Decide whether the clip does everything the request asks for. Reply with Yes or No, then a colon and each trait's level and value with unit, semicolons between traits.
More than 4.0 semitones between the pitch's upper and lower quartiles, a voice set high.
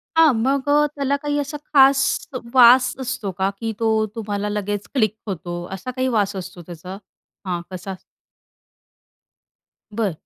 Yes: wide, 5.5 semitones; high, 220 Hz